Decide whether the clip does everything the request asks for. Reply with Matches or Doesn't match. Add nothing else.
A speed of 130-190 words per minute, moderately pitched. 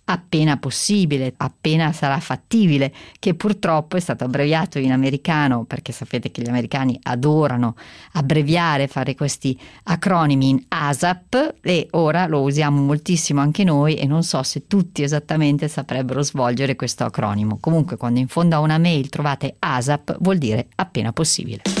Matches